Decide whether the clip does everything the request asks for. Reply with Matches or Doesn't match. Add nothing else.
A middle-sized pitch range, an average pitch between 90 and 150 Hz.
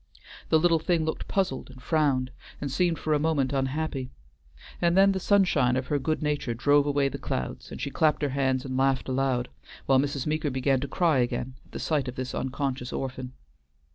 Matches